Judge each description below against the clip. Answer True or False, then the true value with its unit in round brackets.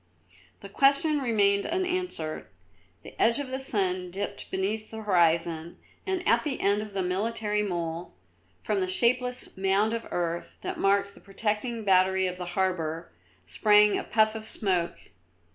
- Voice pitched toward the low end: False (200 Hz)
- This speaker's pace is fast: False (155 wpm)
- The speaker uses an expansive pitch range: False (3.9 semitones)